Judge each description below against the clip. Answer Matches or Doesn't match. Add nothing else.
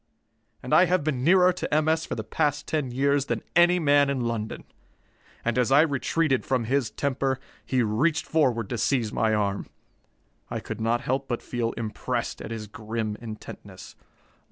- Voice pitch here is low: Matches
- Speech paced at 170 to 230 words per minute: Matches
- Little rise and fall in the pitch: Doesn't match